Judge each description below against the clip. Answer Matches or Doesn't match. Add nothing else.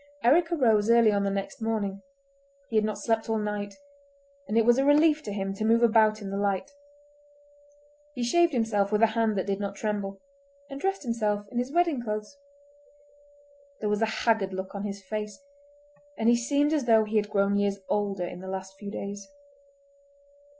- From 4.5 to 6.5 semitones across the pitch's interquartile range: Doesn't match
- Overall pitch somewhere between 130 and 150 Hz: Doesn't match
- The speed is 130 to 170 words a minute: Doesn't match